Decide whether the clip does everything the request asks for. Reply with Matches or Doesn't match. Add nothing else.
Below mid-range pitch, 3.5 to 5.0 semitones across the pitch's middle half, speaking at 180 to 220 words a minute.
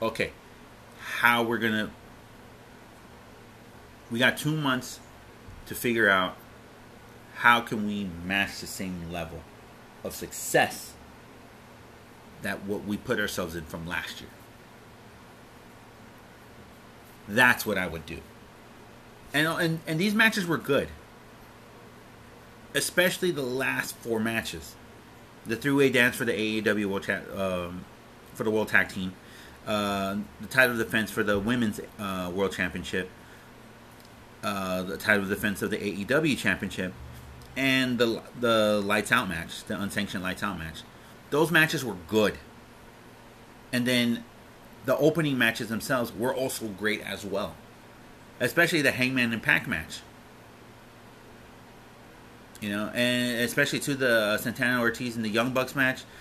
Doesn't match